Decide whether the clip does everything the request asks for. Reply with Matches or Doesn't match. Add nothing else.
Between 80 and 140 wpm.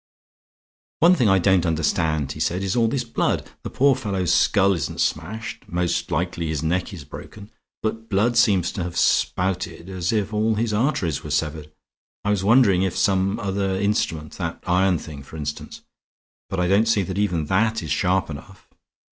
Doesn't match